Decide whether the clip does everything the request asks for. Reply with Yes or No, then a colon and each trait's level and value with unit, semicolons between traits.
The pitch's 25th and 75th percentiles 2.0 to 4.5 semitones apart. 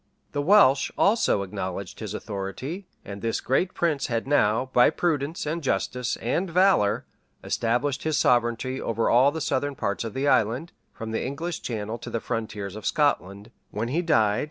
No: average, 5.2 semitones